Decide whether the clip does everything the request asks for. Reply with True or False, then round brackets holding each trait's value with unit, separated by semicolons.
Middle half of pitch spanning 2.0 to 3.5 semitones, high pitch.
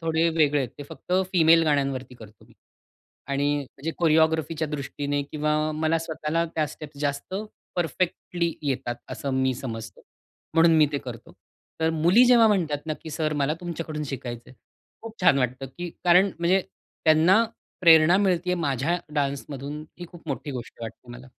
False (3.2 semitones; 155 Hz)